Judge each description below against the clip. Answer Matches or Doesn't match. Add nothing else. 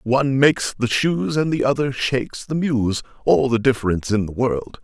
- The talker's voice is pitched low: Matches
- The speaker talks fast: Doesn't match